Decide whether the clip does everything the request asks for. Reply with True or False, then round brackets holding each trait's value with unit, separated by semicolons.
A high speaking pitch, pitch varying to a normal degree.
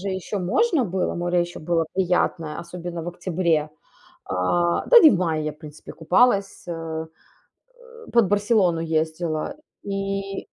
False (175 Hz; 3.3 semitones)